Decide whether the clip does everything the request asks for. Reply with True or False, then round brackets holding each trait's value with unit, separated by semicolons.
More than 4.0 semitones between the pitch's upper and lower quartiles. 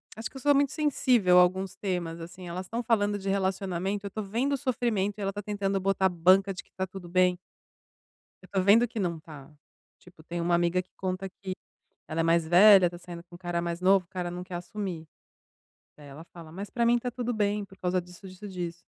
False (2.8 semitones)